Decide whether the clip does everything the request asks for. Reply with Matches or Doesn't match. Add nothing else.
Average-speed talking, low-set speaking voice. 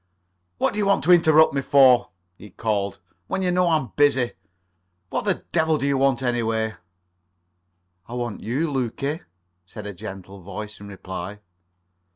Matches